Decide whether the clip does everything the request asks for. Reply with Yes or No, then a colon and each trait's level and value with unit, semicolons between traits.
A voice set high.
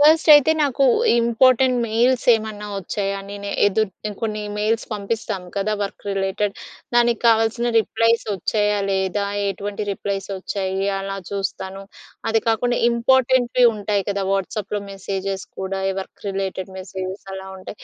Yes: high, 205 Hz